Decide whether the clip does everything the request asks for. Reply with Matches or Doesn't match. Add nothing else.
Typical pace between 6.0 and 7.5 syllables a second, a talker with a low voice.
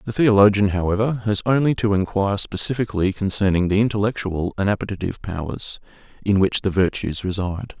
Matches